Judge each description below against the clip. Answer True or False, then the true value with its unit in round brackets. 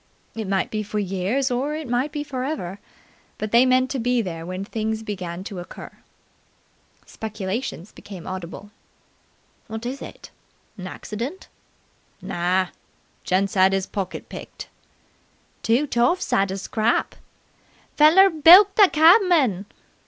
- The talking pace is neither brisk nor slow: False (130 wpm)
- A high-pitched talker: True (220 Hz)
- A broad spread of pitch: True (6.0 semitones)